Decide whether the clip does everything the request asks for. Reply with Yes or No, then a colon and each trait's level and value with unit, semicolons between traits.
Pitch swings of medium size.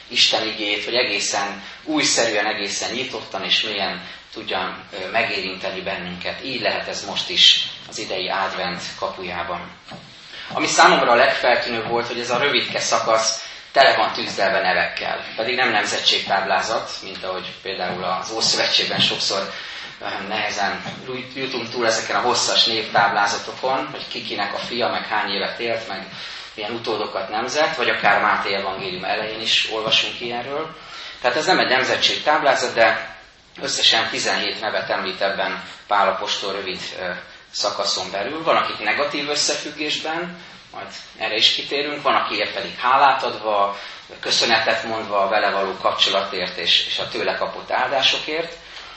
Yes: average, 3.6 semitones